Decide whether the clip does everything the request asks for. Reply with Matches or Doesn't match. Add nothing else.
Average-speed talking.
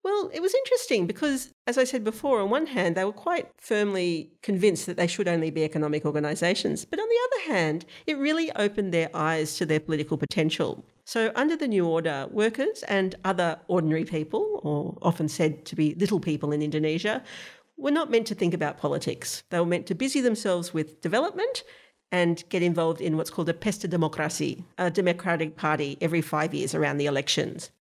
Matches